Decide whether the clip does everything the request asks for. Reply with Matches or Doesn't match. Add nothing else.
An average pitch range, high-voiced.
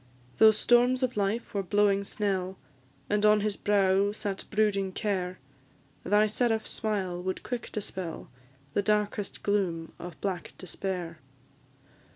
Doesn't match